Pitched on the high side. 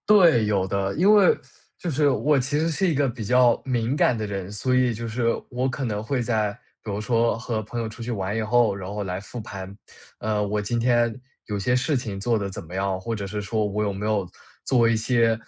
No: low, 115 Hz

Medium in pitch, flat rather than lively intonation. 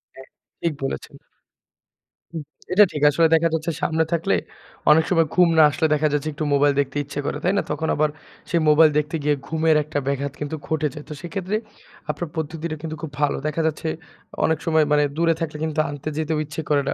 Yes: medium, 155 Hz; narrow, 1.7 semitones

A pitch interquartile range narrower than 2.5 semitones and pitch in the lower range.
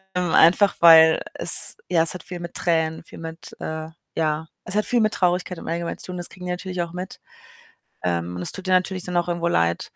No: narrow, 2.0 semitones; medium, 170 Hz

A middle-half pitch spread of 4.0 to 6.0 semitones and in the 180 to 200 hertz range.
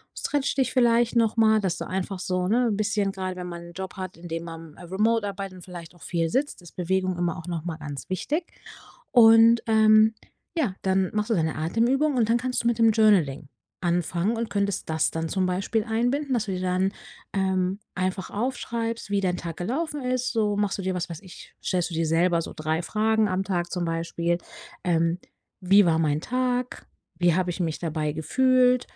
Yes: average, 4.6 semitones; high, 190 Hz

